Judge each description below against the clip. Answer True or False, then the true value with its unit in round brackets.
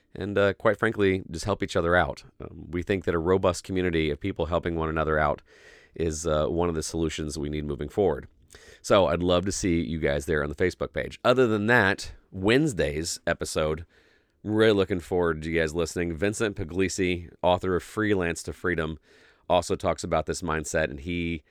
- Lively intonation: False (3.1 semitones)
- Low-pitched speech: True (85 Hz)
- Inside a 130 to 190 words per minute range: False (200 wpm)